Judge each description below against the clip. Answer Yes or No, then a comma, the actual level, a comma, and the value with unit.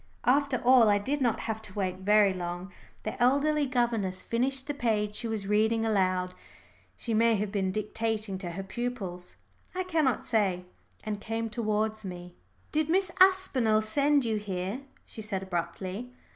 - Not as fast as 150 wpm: No, average, 160 wpm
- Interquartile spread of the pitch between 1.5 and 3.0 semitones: No, average, 4.3 semitones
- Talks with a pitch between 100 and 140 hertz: No, high, 220 Hz